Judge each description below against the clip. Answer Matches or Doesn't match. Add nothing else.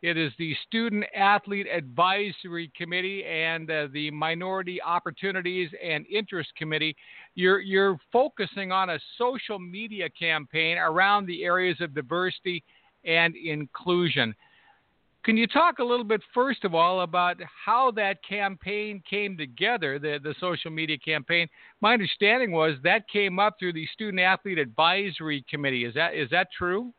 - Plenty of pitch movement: Doesn't match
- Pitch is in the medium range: Matches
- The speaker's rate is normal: Matches